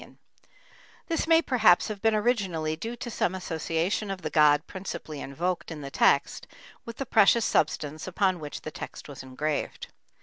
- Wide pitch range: Yes, wide, 5.8 semitones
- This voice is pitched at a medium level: Yes, medium, 180 Hz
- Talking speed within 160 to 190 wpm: Yes, average, 165 wpm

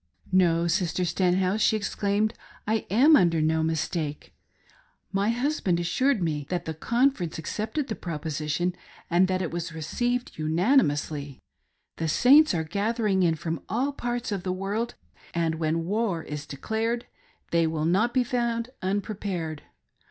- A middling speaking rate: Yes, average, 145 wpm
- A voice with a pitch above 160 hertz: Yes, medium, 185 Hz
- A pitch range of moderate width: No, wide, 5.7 semitones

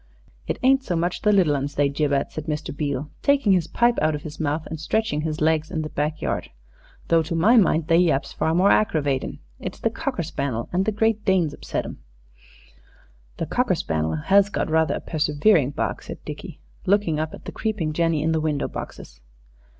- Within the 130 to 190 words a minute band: No, fast, 205 wpm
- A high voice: No, medium, 160 Hz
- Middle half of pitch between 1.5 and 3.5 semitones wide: No, average, 4.2 semitones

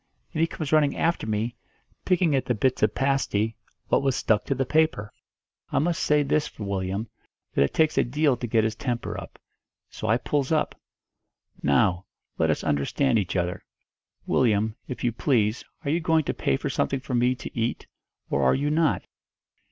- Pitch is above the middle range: No, low, 125 Hz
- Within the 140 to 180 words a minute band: No, average, 190 wpm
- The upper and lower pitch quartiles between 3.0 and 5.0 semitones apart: No, wide, 5.5 semitones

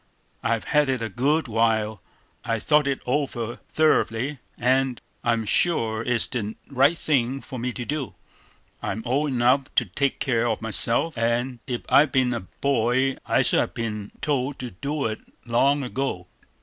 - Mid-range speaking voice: No, low, 125 Hz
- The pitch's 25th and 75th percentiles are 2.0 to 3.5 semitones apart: Yes, average, 3.2 semitones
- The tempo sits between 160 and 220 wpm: Yes, average, 165 wpm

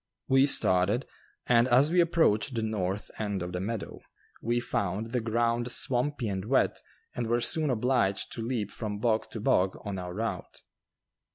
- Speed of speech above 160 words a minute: Yes, average, 170 wpm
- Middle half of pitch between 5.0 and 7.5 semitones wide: No, average, 3.4 semitones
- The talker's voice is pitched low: Yes, low, 115 Hz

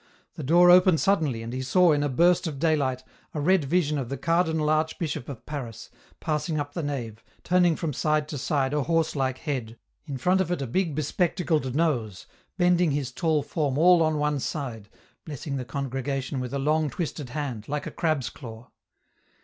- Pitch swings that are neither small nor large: Yes, average, 3.7 semitones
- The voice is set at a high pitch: No, medium, 150 Hz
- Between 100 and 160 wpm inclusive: No, average, 200 wpm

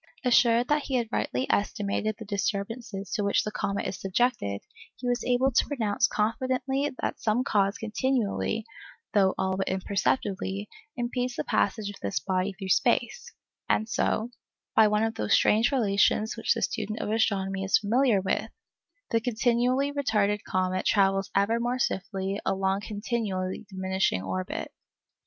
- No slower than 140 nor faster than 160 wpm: Yes, average, 150 wpm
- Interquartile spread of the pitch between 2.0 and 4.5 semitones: Yes, average, 3.8 semitones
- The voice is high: Yes, high, 215 Hz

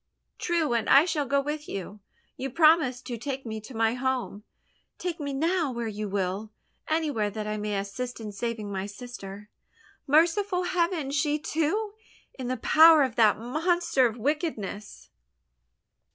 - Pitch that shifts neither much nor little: No, wide, 6.4 semitones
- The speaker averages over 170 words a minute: No, average, 155 wpm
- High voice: Yes, very high, 260 Hz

